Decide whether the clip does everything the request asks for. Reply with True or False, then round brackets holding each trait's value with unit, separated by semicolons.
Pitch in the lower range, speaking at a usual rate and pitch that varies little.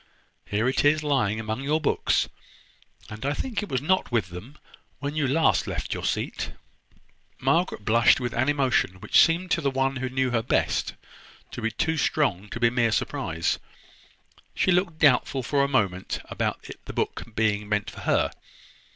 False (130 Hz; 175 wpm; 5.0 semitones)